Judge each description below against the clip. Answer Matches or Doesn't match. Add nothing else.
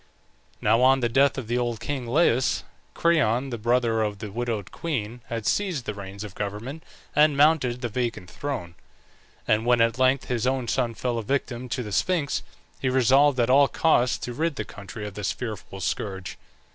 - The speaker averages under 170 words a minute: Doesn't match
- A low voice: Matches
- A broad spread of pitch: Doesn't match